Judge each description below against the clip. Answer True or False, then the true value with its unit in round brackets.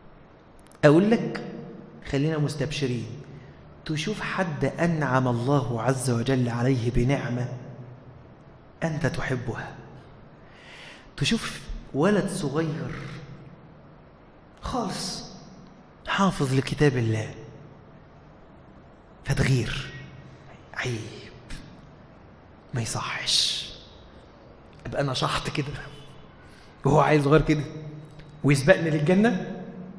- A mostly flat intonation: False (3.8 semitones)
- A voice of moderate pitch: True (145 Hz)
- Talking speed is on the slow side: True (70 wpm)